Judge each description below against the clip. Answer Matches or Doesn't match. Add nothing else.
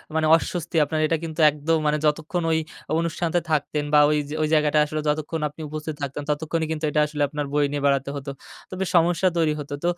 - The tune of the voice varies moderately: Doesn't match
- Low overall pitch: Doesn't match